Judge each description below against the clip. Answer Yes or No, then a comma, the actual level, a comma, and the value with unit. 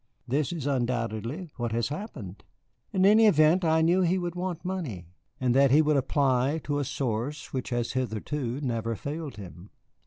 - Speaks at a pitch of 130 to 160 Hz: Yes, medium, 140 Hz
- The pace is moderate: Yes, average, 180 wpm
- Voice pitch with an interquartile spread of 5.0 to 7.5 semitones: Yes, average, 5.3 semitones